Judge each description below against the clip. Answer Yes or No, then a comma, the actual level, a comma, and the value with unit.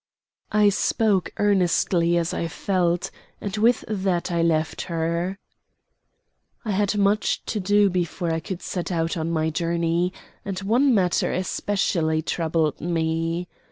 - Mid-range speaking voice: Yes, medium, 175 Hz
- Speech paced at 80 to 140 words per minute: Yes, slow, 135 wpm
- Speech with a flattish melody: No, average, 3.1 semitones